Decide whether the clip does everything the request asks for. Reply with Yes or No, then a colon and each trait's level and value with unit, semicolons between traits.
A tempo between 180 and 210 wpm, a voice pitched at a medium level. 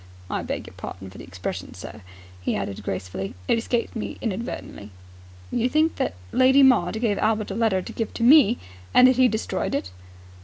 No: average, 190 wpm; high, 220 Hz